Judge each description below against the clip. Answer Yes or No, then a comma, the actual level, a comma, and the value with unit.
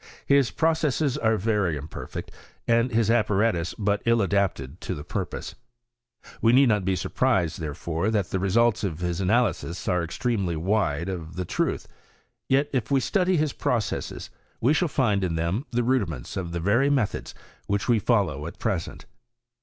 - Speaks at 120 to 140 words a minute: No, average, 165 wpm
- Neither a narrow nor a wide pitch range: No, wide, 5.7 semitones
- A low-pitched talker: Yes, low, 105 Hz